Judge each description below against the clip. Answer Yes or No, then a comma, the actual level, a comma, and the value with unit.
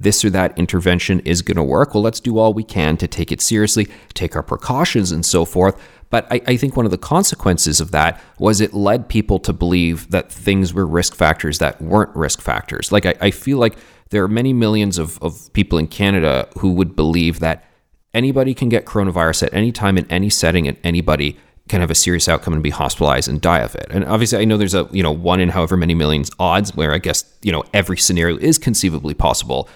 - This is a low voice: Yes, very low, 95 Hz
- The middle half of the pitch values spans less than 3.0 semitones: No, average, 4.4 semitones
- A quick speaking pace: Yes, fast, 230 wpm